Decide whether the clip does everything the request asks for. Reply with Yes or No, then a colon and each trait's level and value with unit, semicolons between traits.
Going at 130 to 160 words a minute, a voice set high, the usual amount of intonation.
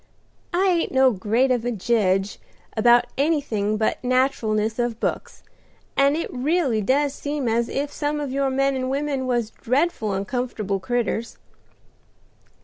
Yes: average, 140 wpm; very high, 255 Hz; average, 4.0 semitones